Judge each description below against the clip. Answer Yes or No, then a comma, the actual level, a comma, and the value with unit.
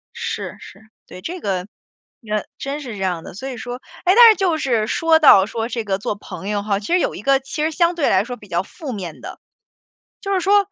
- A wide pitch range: Yes, wide, 8.1 semitones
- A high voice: Yes, high, 245 Hz